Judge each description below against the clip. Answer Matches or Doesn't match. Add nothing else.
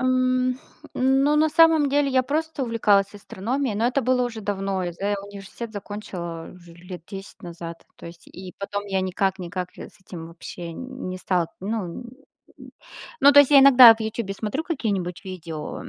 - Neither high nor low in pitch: Doesn't match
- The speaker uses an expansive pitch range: Matches